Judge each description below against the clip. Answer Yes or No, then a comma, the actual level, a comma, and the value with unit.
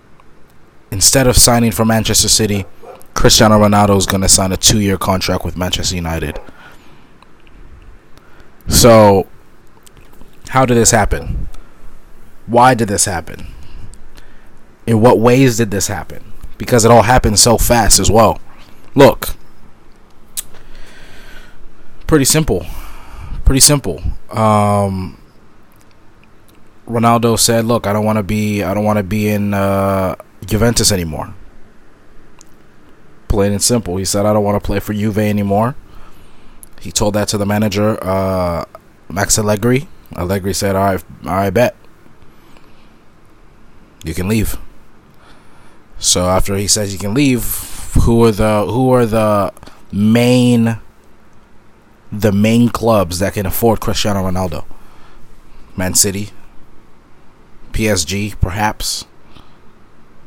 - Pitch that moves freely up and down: No, average, 2.9 semitones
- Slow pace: Yes, slow, 120 wpm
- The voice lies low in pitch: Yes, low, 105 Hz